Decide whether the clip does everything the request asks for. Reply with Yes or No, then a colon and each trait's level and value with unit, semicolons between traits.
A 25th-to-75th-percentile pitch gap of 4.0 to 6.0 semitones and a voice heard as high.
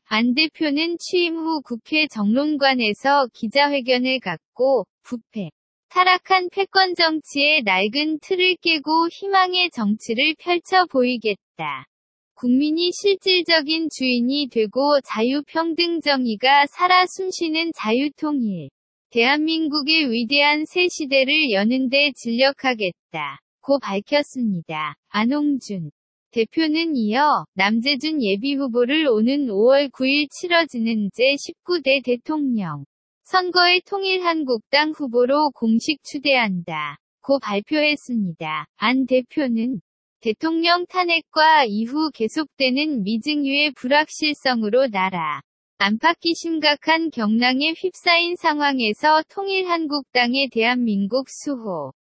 Yes: wide, 5.4 semitones; very high, 280 Hz